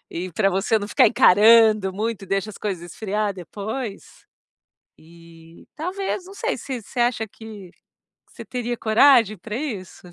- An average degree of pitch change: Yes, average, 3.4 semitones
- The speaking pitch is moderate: No, high, 215 Hz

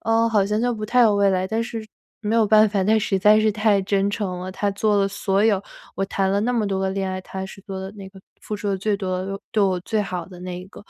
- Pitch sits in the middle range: No, high, 200 Hz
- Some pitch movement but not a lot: No, narrow, 2.1 semitones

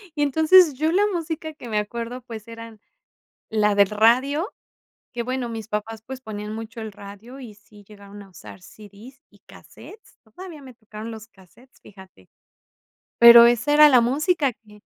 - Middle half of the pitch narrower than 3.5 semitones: No, average, 4.3 semitones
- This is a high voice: Yes, high, 230 Hz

